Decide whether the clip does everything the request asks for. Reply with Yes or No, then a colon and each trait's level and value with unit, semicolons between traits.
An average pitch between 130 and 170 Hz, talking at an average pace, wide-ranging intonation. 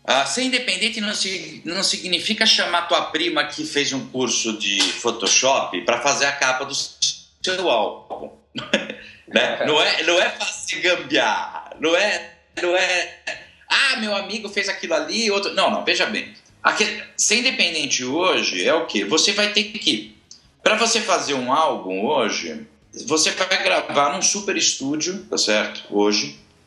No: medium, 180 Hz; average, 160 wpm; wide, 6.9 semitones